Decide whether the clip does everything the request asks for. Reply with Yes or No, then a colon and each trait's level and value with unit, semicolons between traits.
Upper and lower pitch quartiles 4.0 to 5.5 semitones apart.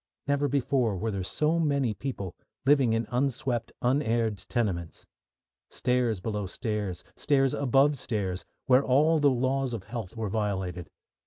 Yes: average, 4.6 semitones